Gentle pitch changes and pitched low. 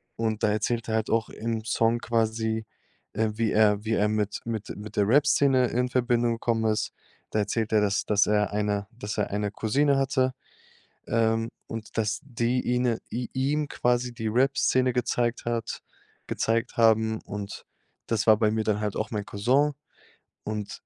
Yes: narrow, 2.2 semitones; low, 115 Hz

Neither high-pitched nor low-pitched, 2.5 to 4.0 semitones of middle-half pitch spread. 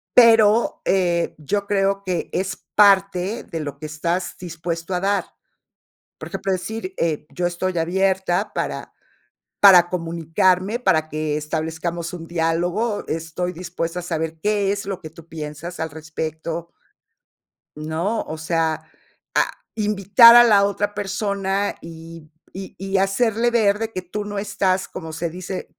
Yes: medium, 180 Hz; average, 3.4 semitones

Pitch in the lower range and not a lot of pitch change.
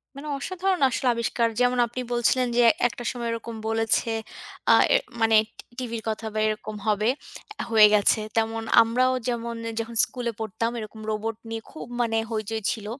No: high, 230 Hz; narrow, 1.5 semitones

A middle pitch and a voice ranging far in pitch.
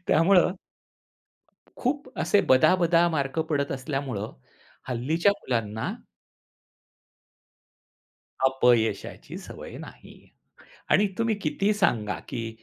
Yes: medium, 145 Hz; wide, 6.9 semitones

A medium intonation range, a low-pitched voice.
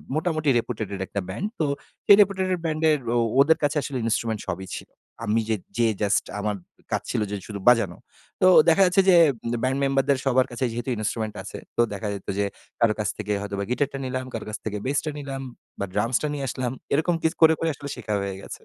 No: wide, 6.2 semitones; low, 130 Hz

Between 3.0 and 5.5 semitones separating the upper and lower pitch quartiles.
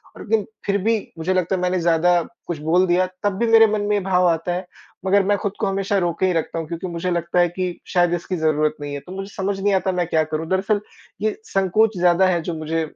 No: narrow, 2.5 semitones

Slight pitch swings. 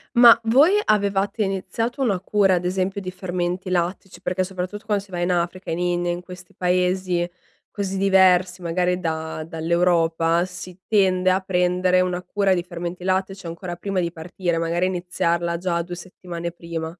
Yes: narrow, 1.6 semitones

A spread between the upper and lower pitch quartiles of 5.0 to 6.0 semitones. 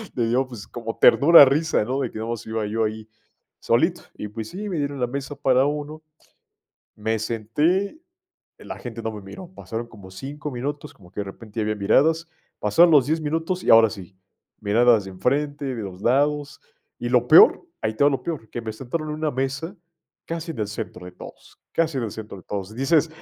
Yes: wide, 5.4 semitones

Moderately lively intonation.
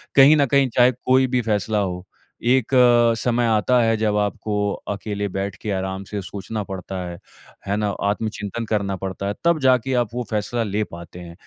Yes: average, 3.6 semitones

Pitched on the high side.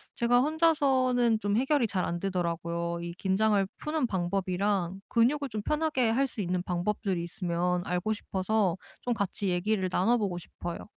Yes: high, 200 Hz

